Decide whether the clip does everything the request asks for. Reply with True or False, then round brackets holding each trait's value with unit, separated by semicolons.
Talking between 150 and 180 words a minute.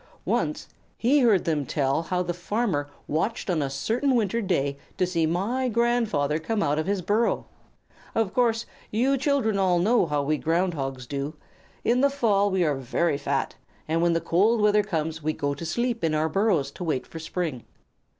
False (190 wpm)